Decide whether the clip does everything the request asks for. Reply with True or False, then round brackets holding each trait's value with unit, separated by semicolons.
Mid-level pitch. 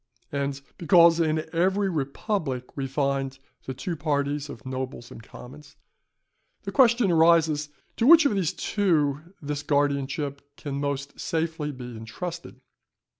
True (145 Hz)